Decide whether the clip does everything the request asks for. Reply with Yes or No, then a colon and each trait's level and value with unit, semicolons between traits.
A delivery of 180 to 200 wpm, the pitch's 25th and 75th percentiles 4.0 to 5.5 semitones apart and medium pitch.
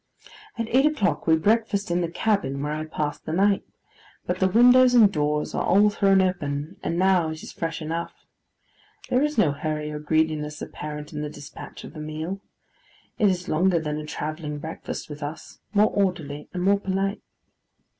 Yes: average, 185 wpm; average, 4.7 semitones; medium, 170 Hz